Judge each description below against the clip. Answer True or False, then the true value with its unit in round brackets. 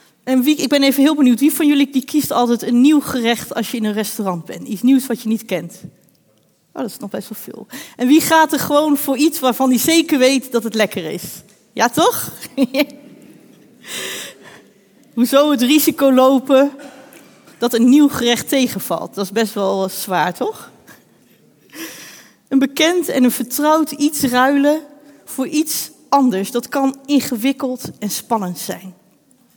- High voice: True (265 Hz)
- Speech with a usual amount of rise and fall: True (4.0 semitones)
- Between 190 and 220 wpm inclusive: False (170 wpm)